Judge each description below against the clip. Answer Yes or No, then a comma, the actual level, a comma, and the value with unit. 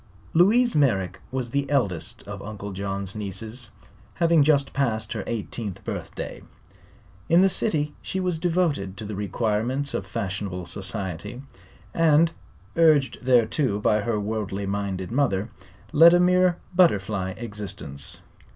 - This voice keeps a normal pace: No, slow, 130 wpm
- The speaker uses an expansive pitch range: Yes, wide, 7.1 semitones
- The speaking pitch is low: Yes, low, 110 Hz